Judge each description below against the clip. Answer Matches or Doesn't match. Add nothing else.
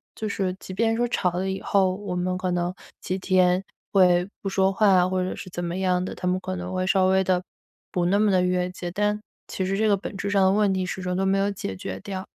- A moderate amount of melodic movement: Doesn't match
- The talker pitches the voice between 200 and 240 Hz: Doesn't match